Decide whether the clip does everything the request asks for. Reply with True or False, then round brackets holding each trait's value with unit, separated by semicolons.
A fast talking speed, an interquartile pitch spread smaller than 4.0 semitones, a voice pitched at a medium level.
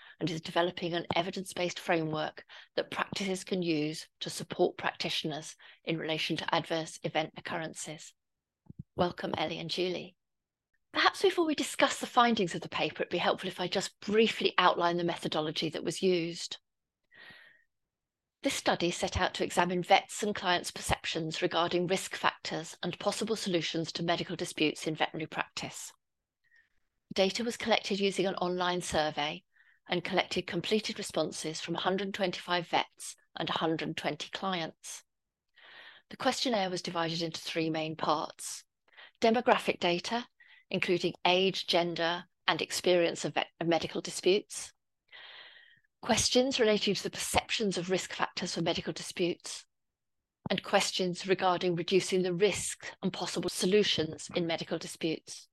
False (140 wpm; 2.8 semitones; 180 Hz)